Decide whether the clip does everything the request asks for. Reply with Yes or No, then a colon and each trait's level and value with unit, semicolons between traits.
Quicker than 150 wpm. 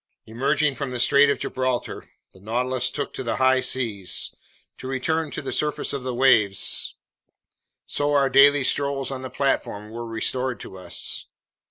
Yes: average, 165 wpm